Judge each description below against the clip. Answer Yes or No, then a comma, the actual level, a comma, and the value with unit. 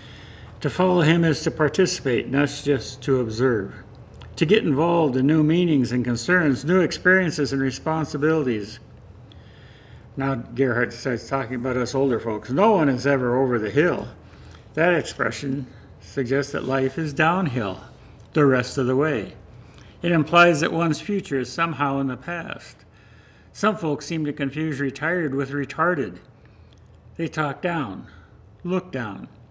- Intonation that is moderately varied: Yes, average, 4.7 semitones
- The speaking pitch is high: No, medium, 140 Hz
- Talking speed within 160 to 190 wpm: No, average, 145 wpm